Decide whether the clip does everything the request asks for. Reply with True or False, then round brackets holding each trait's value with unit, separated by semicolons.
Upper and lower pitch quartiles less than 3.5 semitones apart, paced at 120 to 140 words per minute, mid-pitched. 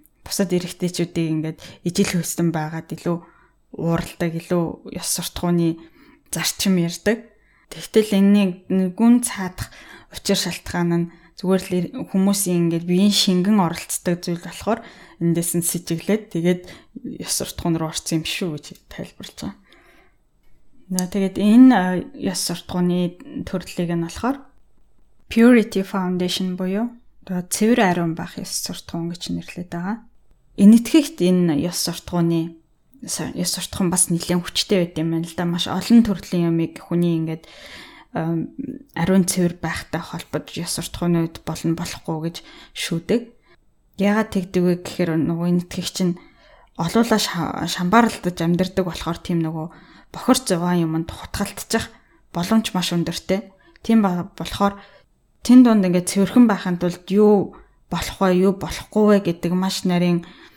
True (2.8 semitones; 130 wpm; 180 Hz)